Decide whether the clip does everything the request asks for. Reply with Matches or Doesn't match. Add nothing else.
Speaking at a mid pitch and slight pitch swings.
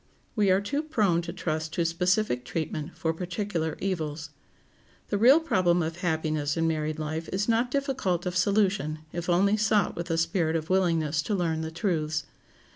Doesn't match